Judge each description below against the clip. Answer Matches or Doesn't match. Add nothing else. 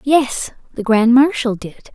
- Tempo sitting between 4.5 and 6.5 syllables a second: Doesn't match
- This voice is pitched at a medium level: Doesn't match